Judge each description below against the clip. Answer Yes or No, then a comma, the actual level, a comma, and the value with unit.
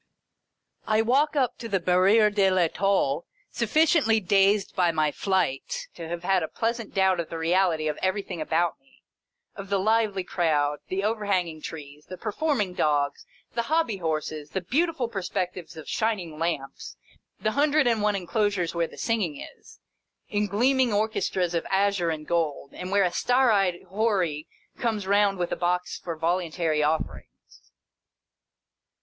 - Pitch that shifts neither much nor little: Yes, average, 4.5 semitones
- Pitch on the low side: No, high, 190 Hz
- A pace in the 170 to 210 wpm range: No, average, 155 wpm